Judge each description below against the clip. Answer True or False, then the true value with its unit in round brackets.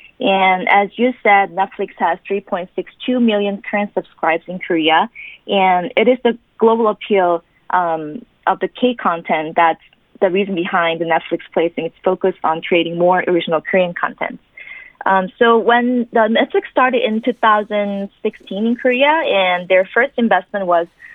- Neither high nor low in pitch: False (200 Hz)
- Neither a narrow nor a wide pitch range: True (4.7 semitones)